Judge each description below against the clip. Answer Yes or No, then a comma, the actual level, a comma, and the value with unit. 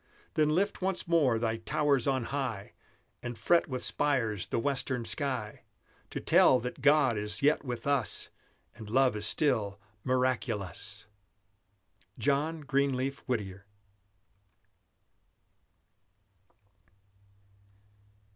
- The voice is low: Yes, low, 130 Hz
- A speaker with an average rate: No, slow, 100 wpm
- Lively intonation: No, average, 4.2 semitones